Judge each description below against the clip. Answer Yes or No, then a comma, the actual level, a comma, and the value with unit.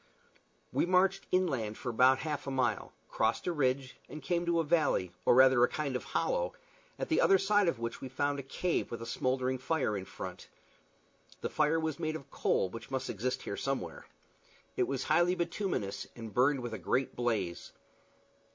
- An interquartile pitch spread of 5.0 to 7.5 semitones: Yes, wide, 5.4 semitones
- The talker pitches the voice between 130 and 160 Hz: Yes, low, 135 Hz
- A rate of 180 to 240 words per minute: Yes, average, 190 wpm